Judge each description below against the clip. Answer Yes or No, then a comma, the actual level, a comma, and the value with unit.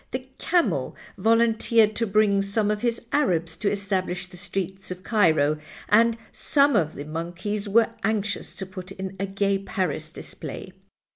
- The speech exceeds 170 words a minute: No, average, 155 wpm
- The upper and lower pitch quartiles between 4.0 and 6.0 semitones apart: No, average, 3.1 semitones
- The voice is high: Yes, high, 200 Hz